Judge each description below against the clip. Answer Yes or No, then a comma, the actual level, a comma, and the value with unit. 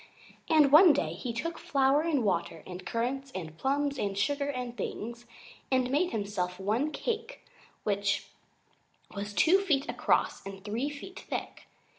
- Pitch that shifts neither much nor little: No, wide, 6.3 semitones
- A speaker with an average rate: Yes, average, 150 wpm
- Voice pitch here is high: Yes, very high, 255 Hz